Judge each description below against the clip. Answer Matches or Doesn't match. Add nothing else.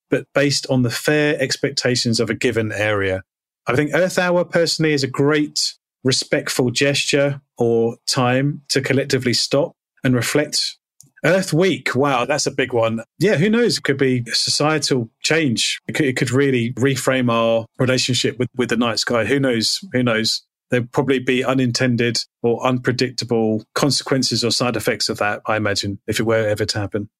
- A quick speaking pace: Doesn't match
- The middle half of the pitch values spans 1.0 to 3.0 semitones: Doesn't match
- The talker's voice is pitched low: Matches